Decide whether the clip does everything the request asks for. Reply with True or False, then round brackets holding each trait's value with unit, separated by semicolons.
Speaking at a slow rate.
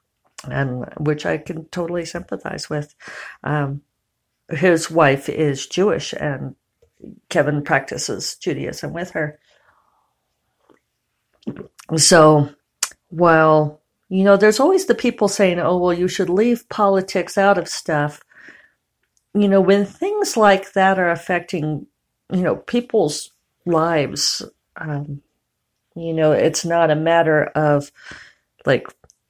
True (115 wpm)